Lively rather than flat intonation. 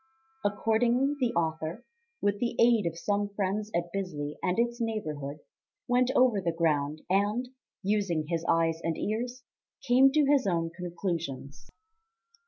Yes: wide, 6.1 semitones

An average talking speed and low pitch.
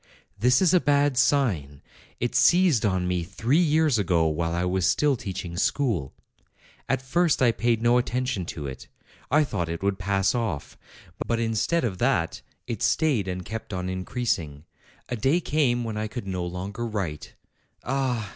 Yes: average, 170 wpm; low, 110 Hz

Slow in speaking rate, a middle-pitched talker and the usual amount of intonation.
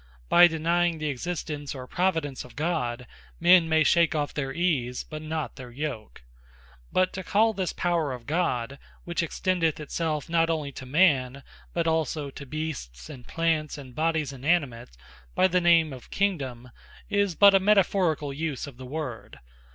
No: average, 165 wpm; medium, 155 Hz; average, 4.2 semitones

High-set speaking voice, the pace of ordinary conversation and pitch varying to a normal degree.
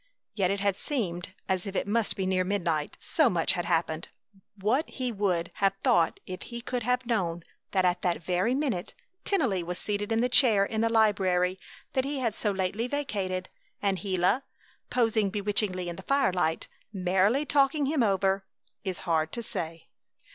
Yes: high, 195 Hz; average, 175 wpm; average, 4.3 semitones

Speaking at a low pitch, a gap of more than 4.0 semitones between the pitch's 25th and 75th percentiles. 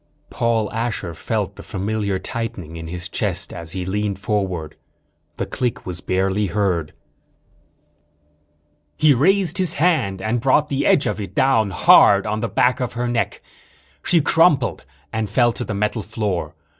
Yes: low, 105 Hz; average, 4.5 semitones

